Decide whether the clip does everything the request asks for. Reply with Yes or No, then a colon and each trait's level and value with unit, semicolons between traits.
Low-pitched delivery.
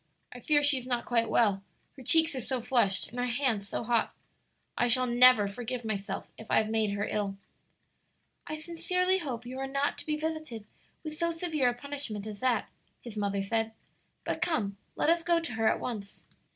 No: high, 245 Hz